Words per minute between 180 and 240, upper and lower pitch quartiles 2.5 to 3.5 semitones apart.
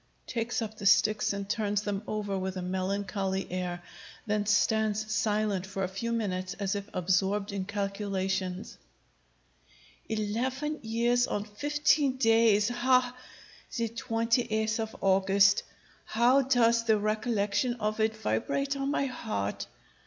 No: slow, 135 wpm; average, 2.8 semitones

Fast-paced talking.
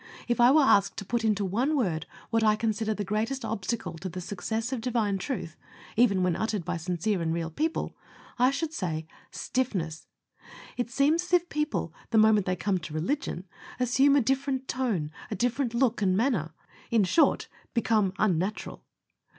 No: average, 175 wpm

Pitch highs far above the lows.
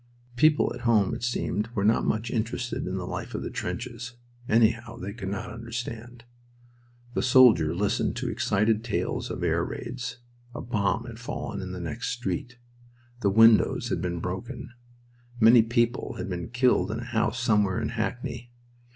No: average, 2.9 semitones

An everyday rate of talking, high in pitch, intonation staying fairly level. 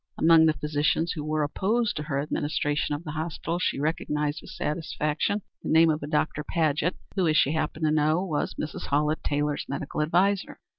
No: average, 190 wpm; medium, 155 Hz; narrow, 1.9 semitones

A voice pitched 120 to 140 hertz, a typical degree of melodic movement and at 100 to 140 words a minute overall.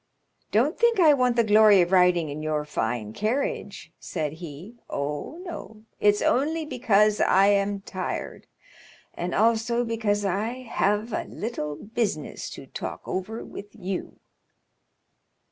No: high, 205 Hz; average, 4.6 semitones; slow, 135 wpm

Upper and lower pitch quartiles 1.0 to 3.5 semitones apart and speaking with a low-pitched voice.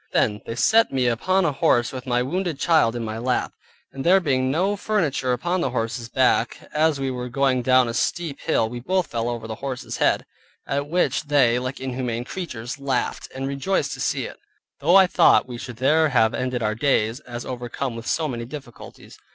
No: average, 3.9 semitones; low, 130 Hz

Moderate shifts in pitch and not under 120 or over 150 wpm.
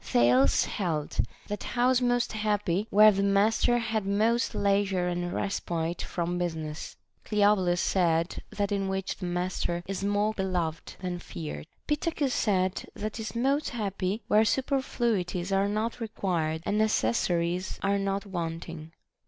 Yes: average, 3.5 semitones; average, 140 wpm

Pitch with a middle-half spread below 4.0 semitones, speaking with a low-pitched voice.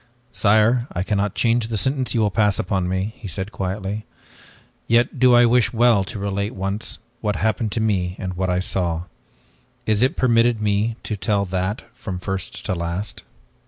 Yes: average, 3.3 semitones; low, 105 Hz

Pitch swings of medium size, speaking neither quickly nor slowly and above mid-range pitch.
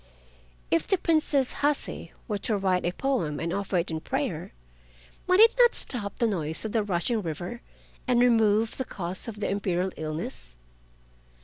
No: wide, 5.9 semitones; average, 170 wpm; high, 205 Hz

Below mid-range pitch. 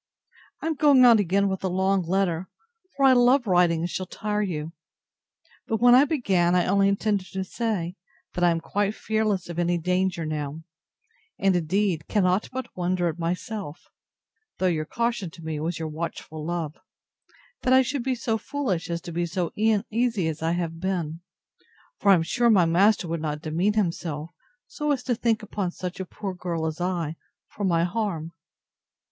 No: medium, 185 Hz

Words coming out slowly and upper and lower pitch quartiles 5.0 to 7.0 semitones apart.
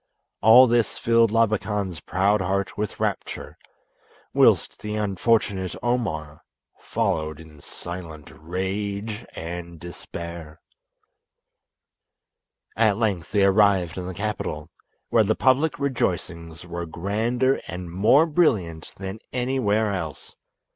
No: slow, 105 wpm; average, 4.5 semitones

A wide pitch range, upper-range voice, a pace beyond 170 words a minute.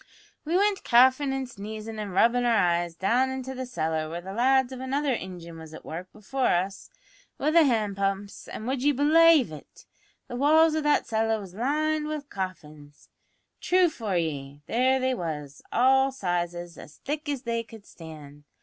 Yes: wide, 7.4 semitones; high, 230 Hz; average, 185 wpm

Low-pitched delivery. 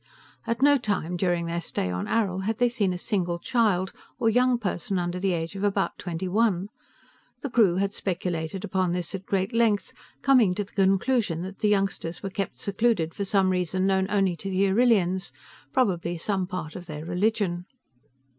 No: high, 190 Hz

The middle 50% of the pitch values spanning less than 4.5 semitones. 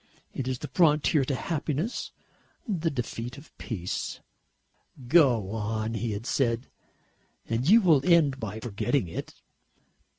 No: average, 5.1 semitones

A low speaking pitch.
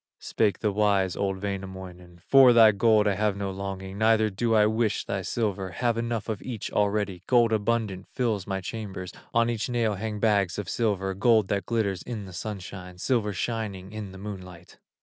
Yes: low, 105 Hz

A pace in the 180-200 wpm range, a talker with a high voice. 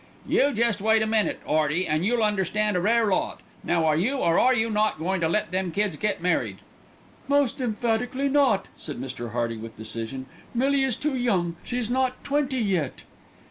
Yes: average, 185 wpm; high, 210 Hz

